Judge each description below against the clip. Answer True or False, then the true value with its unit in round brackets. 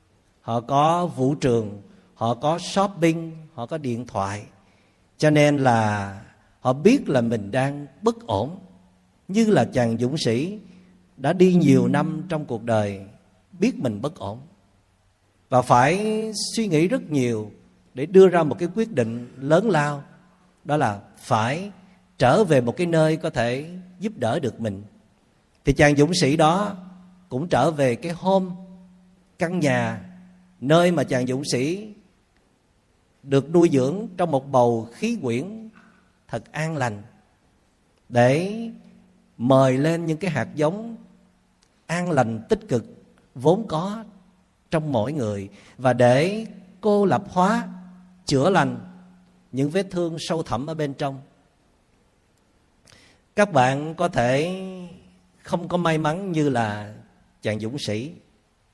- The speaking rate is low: True (140 wpm)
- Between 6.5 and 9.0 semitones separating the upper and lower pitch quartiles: True (7.7 semitones)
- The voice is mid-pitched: True (145 Hz)